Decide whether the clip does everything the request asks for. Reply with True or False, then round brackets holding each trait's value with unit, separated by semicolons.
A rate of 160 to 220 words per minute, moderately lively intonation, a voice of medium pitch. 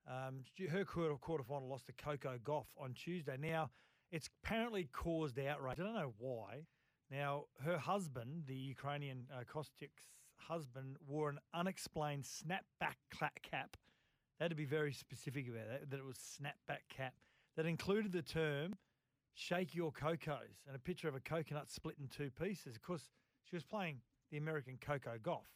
True (165 wpm; 3.4 semitones; 145 Hz)